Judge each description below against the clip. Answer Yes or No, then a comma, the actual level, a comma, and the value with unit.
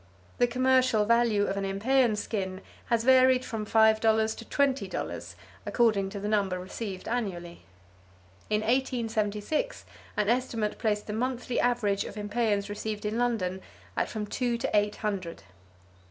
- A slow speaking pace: No, average, 150 wpm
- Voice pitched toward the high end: Yes, high, 220 Hz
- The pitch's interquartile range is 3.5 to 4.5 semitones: No, average, 2.8 semitones